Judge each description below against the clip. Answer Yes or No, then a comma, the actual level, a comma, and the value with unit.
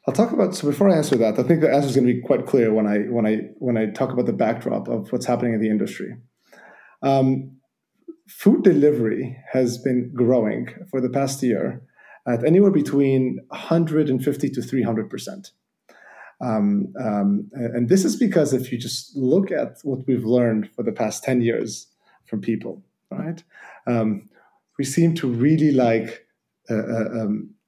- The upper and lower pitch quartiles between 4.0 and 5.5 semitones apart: Yes, average, 4.3 semitones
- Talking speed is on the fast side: No, average, 175 wpm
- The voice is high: No, low, 130 Hz